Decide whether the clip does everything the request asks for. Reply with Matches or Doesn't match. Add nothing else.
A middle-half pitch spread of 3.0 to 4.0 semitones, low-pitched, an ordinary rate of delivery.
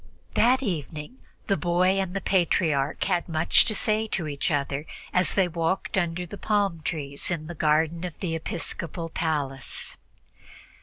Doesn't match